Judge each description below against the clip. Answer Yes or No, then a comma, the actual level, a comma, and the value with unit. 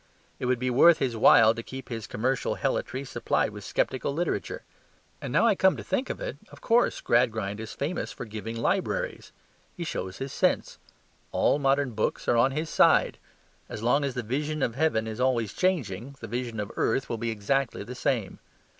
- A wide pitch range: No, average, 3.8 semitones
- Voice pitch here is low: Yes, low, 125 Hz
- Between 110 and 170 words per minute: No, average, 195 wpm